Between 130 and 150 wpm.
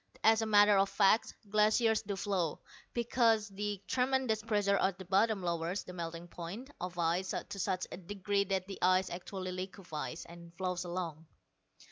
No: average, 165 wpm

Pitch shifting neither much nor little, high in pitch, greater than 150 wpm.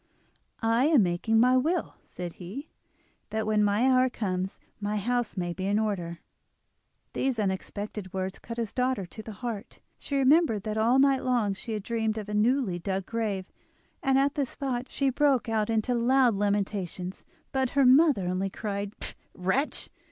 Yes: average, 4.5 semitones; high, 220 Hz; average, 170 wpm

